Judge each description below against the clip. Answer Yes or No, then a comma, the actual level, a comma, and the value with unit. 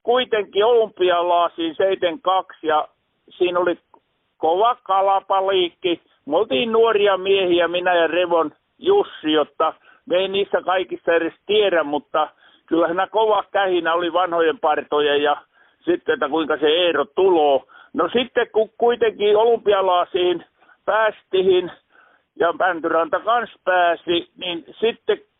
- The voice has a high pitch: Yes, high, 195 Hz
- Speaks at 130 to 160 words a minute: No, average, 120 wpm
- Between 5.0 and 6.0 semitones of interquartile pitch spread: Yes, average, 5.3 semitones